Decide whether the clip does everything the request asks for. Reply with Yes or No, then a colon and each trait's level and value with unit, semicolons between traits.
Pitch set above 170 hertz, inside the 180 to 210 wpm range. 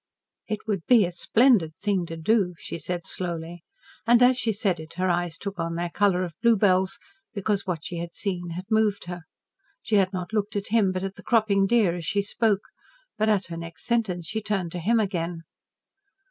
Yes: high, 190 Hz; fast, 205 wpm